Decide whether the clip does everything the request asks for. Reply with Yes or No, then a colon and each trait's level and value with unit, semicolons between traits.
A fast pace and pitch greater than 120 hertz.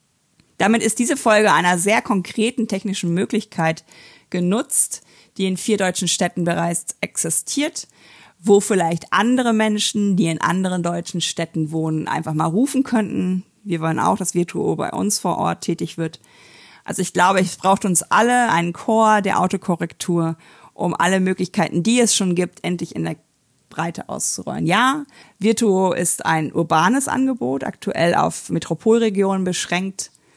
No: average, 150 wpm; medium, 185 Hz